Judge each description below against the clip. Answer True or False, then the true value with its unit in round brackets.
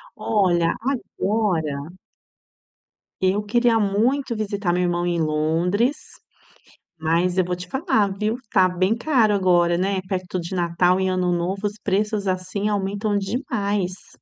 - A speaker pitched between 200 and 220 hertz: False (190 Hz)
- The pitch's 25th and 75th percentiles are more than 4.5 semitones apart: False (2.9 semitones)